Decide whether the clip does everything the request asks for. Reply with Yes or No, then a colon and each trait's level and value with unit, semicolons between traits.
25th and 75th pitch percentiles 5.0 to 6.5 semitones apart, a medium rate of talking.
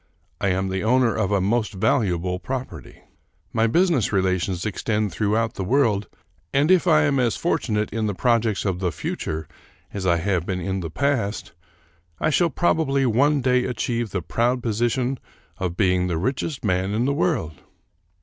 Yes: wide, 5.5 semitones; average, 170 wpm